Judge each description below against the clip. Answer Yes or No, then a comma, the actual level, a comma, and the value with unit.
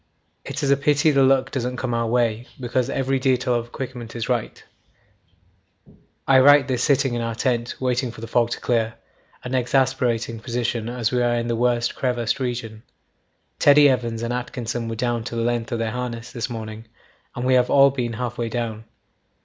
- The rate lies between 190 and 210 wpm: Yes, average, 195 wpm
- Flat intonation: Yes, narrow, 1.8 semitones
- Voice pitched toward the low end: Yes, low, 120 Hz